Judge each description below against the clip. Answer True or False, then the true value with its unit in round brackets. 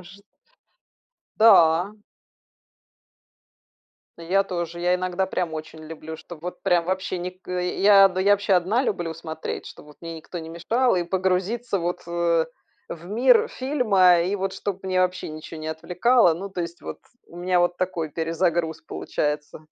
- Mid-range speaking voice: True (180 Hz)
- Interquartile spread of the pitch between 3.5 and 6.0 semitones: False (2.5 semitones)